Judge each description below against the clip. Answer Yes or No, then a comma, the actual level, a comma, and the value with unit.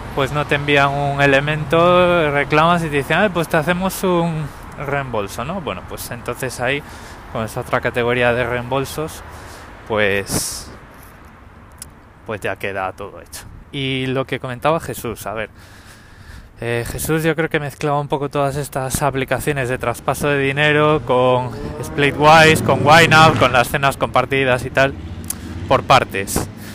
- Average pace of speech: Yes, average, 150 wpm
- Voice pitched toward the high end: No, low, 130 Hz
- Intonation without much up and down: No, average, 5.2 semitones